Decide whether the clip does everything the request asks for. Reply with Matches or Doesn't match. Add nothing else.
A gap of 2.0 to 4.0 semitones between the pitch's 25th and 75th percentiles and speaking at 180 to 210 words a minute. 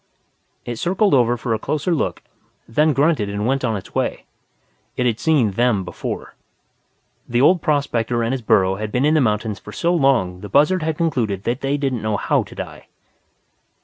Doesn't match